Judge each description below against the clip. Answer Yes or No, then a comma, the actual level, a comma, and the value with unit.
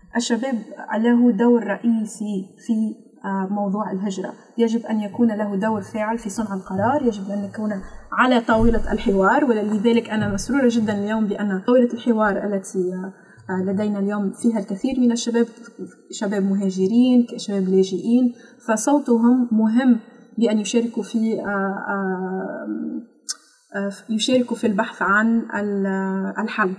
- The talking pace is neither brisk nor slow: Yes, average, 115 wpm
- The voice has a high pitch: Yes, high, 215 Hz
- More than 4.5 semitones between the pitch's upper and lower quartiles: No, average, 2.8 semitones